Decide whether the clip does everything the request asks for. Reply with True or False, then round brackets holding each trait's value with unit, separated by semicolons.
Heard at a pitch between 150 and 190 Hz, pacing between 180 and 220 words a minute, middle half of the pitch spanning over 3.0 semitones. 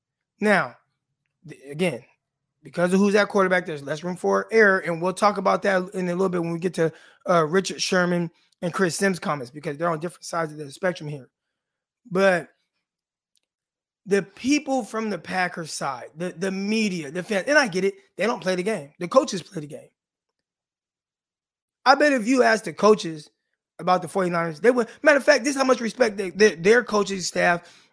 True (185 Hz; 200 wpm; 3.8 semitones)